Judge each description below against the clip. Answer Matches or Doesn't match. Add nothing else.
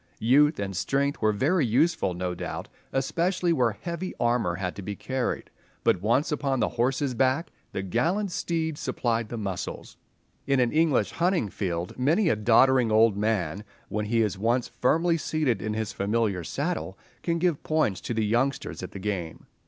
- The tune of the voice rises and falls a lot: Matches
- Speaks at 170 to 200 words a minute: Matches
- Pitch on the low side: Matches